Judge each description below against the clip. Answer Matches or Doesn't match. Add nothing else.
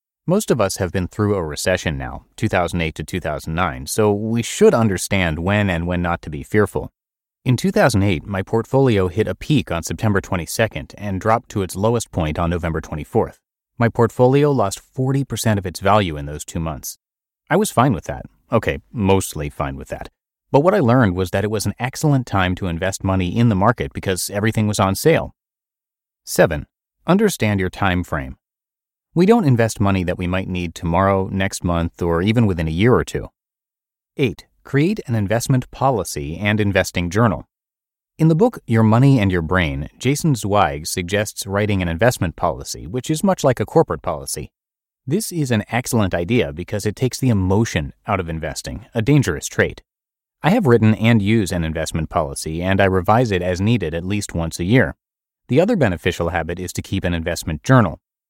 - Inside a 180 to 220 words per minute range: Matches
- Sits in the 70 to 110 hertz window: Matches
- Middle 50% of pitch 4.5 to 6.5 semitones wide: Matches